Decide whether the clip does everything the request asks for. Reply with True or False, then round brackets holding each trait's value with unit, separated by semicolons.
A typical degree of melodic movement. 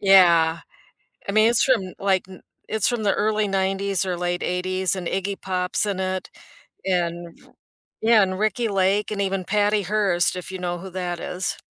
False (2.1 semitones)